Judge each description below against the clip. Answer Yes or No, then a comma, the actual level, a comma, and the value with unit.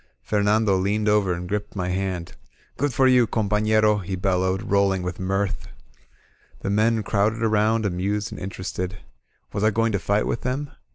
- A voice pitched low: Yes, low, 100 Hz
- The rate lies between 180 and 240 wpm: No, average, 170 wpm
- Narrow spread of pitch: Yes, narrow, 2.3 semitones